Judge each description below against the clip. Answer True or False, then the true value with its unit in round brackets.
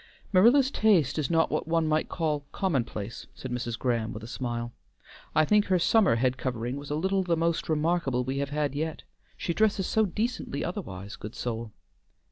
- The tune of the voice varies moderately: False (6.6 semitones)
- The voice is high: False (150 Hz)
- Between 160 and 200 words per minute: True (185 wpm)